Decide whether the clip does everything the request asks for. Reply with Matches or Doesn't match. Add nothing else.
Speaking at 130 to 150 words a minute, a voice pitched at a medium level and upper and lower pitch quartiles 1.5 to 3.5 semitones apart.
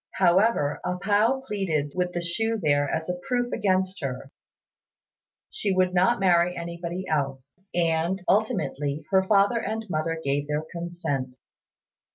Doesn't match